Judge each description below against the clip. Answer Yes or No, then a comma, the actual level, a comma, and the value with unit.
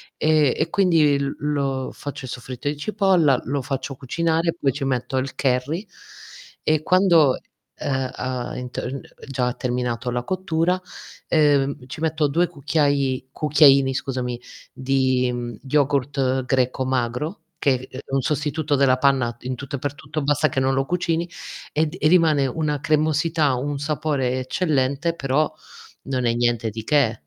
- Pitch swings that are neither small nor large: Yes, average, 3.1 semitones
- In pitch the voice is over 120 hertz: Yes, medium, 140 Hz